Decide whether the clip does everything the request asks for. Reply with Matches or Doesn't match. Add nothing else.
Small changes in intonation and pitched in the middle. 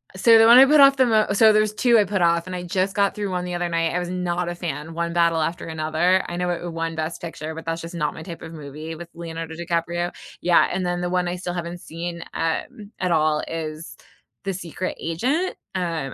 Matches